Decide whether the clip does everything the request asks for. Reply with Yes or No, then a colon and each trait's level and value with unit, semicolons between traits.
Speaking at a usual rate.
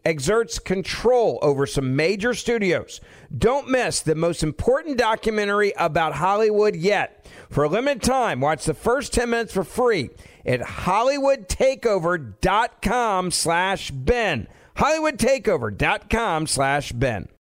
No: slow, 105 wpm